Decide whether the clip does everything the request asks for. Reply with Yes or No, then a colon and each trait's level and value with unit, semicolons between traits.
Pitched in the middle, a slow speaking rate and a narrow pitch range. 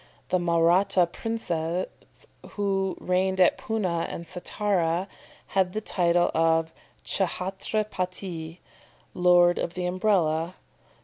Yes: medium, 180 Hz; slow, 105 wpm; narrow, 2.1 semitones